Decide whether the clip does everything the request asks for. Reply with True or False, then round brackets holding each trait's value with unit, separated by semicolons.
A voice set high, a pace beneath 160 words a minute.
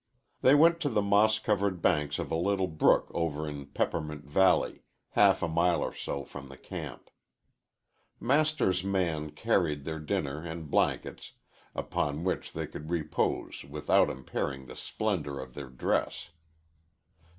False (80 Hz; 145 wpm)